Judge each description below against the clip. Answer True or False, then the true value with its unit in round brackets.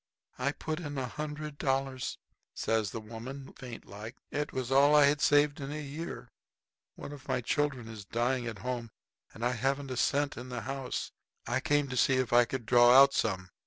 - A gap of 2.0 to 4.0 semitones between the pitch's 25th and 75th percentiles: True (3.1 semitones)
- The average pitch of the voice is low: True (130 Hz)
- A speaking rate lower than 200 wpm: False (205 wpm)